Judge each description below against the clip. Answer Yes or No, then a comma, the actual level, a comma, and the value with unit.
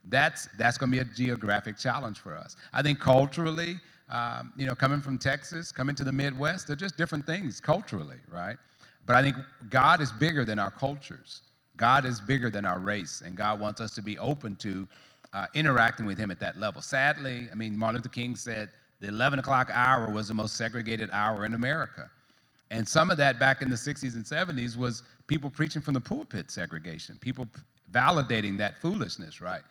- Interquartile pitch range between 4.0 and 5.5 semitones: Yes, average, 4.3 semitones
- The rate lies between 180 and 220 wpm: Yes, average, 200 wpm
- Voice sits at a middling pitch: No, low, 125 Hz